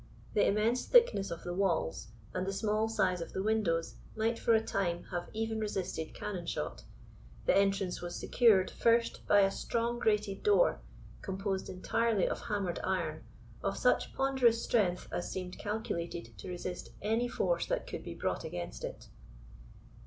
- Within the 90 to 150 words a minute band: No, average, 160 wpm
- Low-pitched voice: No, high, 200 Hz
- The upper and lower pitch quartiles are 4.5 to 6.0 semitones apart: No, average, 3.8 semitones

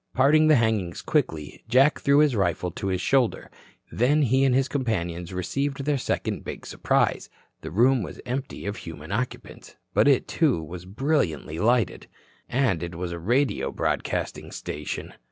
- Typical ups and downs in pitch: No, wide, 7.5 semitones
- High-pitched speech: No, low, 115 Hz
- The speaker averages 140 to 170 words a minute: Yes, average, 160 wpm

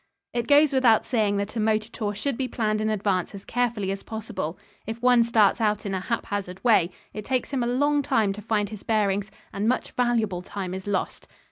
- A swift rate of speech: Yes, fast, 215 wpm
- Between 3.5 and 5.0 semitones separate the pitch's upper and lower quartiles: No, average, 3.0 semitones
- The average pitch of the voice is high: Yes, high, 215 Hz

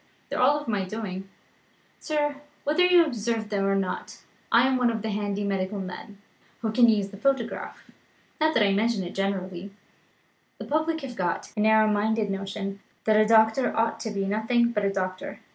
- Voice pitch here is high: Yes, high, 215 Hz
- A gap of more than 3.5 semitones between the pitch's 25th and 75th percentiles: No, average, 3.2 semitones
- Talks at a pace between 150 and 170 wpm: No, average, 190 wpm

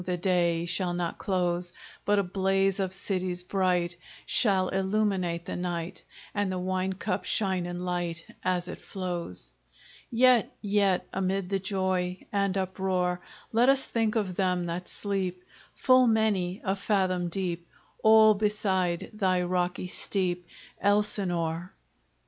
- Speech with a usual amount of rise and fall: No, narrow, 1.9 semitones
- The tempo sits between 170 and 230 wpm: No, slow, 135 wpm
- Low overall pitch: No, medium, 185 Hz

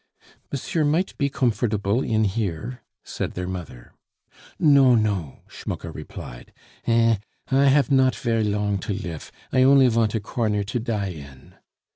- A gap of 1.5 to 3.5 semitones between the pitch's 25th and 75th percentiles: No, average, 4.5 semitones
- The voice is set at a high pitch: No, low, 110 Hz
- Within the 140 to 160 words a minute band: Yes, average, 145 wpm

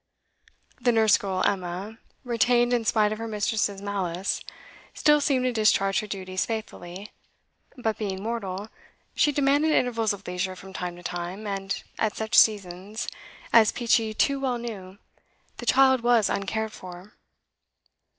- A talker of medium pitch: No, high, 215 Hz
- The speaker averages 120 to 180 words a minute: Yes, average, 145 wpm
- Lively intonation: No, average, 3.5 semitones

